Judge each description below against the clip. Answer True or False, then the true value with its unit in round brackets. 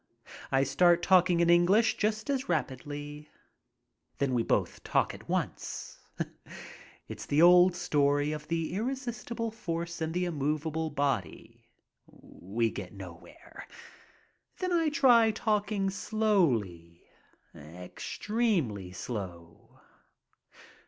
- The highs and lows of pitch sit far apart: True (7.5 semitones)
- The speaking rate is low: True (105 wpm)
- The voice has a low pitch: False (170 Hz)